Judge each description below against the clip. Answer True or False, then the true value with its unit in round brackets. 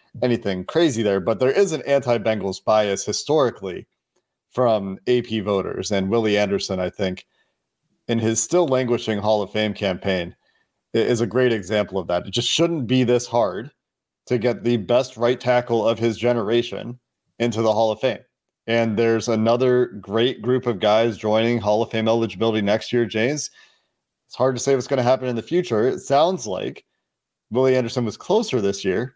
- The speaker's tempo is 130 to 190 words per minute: True (180 wpm)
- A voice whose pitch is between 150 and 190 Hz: False (115 Hz)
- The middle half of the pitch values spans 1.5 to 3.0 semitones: True (2.7 semitones)